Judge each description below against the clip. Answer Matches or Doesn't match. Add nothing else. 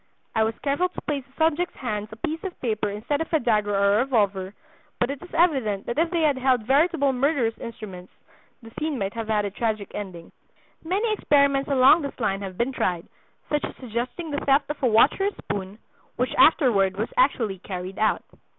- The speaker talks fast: Matches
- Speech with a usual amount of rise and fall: Doesn't match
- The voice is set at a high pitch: Matches